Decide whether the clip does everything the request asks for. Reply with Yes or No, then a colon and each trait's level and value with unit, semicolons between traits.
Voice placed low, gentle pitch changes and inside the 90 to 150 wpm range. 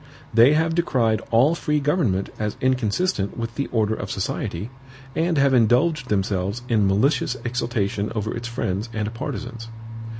No: low, 115 Hz; average, 4.5 semitones; average, 145 wpm